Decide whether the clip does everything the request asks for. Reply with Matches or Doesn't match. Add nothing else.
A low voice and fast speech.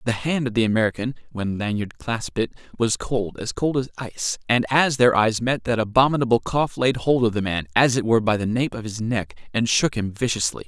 Matches